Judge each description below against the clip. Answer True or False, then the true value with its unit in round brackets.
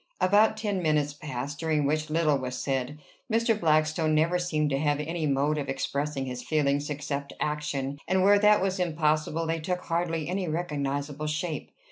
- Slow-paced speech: False (170 wpm)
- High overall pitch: False (155 Hz)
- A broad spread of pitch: False (2.9 semitones)